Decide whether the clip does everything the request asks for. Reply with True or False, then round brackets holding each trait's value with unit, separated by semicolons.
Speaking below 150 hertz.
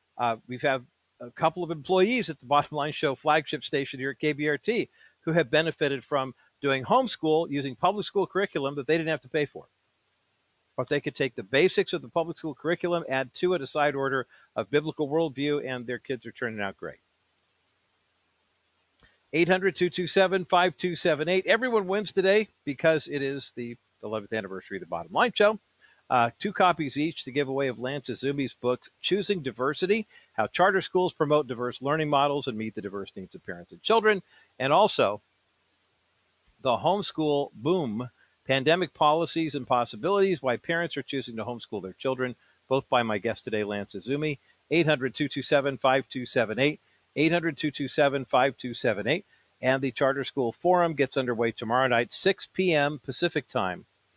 True (140 Hz)